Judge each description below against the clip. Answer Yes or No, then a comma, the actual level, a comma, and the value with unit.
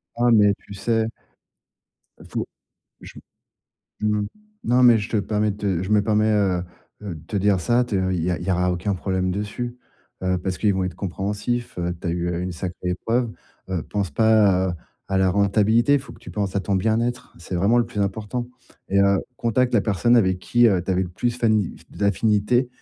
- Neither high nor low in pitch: No, low, 100 Hz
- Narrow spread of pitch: No, average, 3.3 semitones